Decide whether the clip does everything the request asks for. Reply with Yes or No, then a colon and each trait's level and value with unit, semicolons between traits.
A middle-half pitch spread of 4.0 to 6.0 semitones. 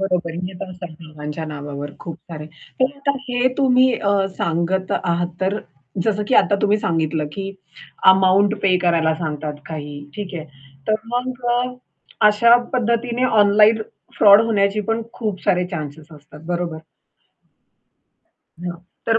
Yes: average, 5.1 semitones